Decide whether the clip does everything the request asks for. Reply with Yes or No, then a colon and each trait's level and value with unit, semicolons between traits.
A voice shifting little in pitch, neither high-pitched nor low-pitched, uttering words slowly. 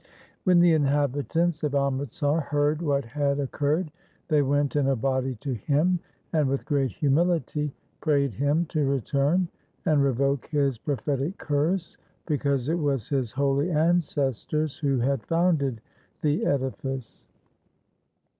Yes: narrow, 2.1 semitones; medium, 145 Hz; slow, 130 wpm